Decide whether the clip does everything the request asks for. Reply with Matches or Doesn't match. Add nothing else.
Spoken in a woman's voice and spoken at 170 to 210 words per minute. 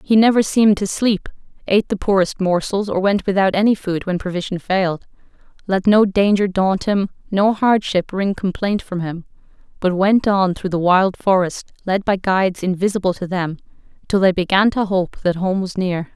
Matches